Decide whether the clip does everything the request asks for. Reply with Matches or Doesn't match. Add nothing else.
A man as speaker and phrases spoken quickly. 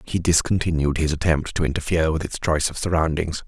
Doesn't match